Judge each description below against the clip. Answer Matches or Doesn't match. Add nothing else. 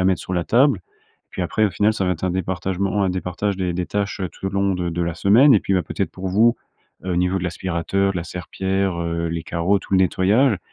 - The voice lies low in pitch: Matches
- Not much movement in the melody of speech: Matches